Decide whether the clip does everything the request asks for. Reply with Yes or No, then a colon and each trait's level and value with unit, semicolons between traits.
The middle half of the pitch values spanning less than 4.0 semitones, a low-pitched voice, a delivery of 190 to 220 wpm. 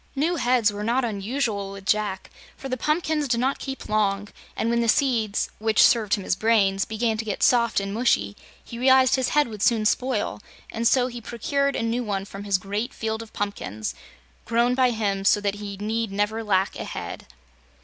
No: average, 3.4 semitones; high, 225 Hz; average, 200 wpm